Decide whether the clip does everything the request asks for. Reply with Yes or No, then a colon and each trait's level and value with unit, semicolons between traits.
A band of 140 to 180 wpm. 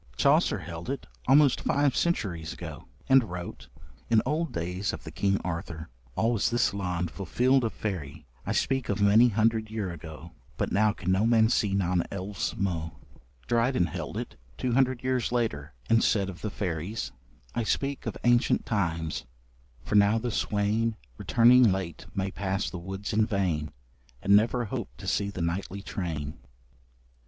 Yes: average, 165 wpm